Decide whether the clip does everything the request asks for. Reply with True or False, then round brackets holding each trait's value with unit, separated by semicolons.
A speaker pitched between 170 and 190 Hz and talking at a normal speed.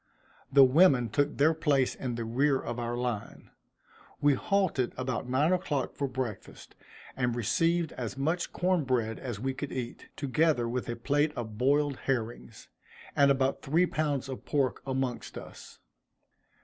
False (135 Hz; 155 wpm)